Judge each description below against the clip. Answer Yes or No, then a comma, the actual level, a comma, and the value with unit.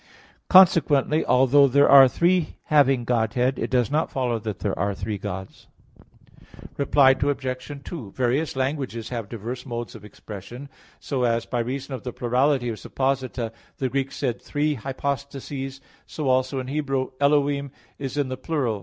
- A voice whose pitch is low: Yes, low, 130 Hz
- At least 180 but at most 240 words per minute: No, average, 155 wpm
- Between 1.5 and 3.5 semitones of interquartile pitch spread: Yes, average, 2.7 semitones